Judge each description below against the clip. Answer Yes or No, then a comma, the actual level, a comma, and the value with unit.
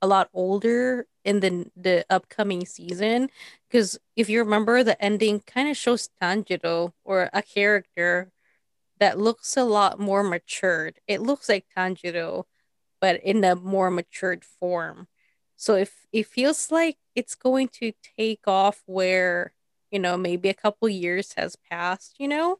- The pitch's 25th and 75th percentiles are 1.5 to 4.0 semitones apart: Yes, average, 3.7 semitones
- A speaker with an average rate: Yes, average, 155 wpm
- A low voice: No, high, 200 Hz